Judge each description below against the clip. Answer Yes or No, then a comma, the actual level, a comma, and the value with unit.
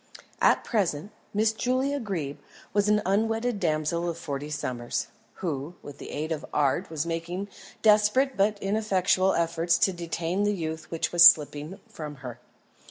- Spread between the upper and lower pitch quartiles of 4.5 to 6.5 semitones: Yes, average, 5.0 semitones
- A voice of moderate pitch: Yes, medium, 175 Hz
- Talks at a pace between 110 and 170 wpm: Yes, average, 155 wpm